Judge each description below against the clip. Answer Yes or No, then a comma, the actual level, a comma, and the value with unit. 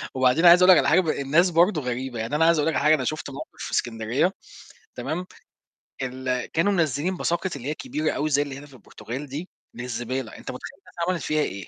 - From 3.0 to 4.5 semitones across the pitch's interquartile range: No, average, 4.9 semitones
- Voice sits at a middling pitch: Yes, medium, 145 Hz